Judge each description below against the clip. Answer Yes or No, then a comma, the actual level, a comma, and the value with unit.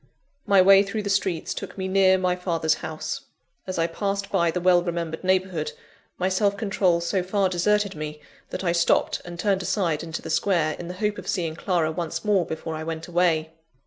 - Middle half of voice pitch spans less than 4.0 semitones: Yes, average, 2.9 semitones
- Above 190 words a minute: Yes, fast, 205 wpm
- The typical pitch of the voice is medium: Yes, medium, 180 Hz